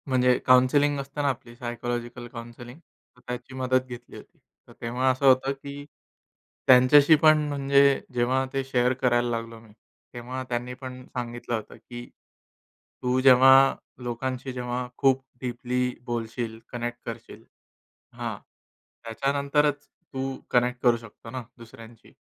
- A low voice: Yes, low, 125 Hz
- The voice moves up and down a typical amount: No, narrow, 1.7 semitones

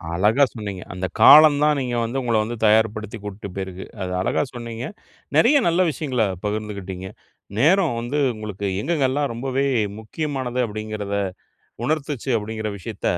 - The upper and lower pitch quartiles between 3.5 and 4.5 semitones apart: No, average, 4.9 semitones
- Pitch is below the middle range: Yes, low, 115 Hz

